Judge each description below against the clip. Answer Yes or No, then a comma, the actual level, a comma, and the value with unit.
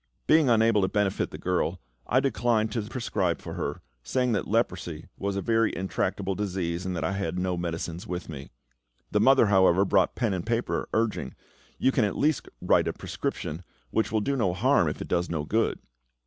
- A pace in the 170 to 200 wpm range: Yes, average, 195 wpm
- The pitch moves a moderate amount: Yes, average, 4.2 semitones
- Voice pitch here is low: Yes, low, 100 Hz